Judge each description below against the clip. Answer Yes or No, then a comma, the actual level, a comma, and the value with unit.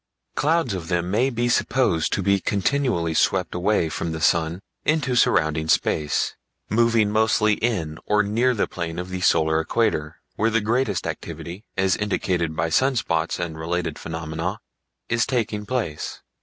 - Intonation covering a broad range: Yes, wide, 5.7 semitones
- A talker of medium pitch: No, very low, 95 Hz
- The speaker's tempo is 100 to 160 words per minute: Yes, average, 155 wpm